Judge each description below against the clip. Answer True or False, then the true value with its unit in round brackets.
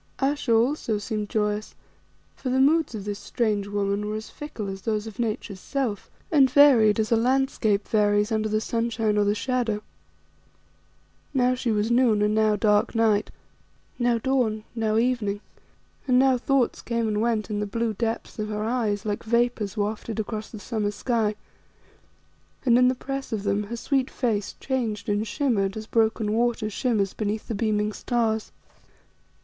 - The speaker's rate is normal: True (170 wpm)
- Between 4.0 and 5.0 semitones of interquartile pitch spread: False (2.5 semitones)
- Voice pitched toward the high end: True (220 Hz)